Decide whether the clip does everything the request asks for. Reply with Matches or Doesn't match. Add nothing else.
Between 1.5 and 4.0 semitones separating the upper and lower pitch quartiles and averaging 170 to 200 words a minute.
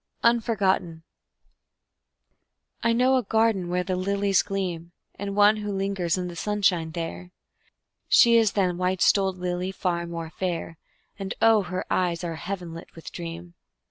Doesn't match